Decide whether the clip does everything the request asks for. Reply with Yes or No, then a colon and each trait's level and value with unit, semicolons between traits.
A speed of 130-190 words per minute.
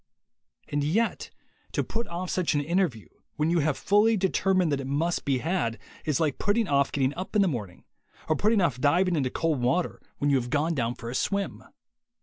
No: fast, 205 wpm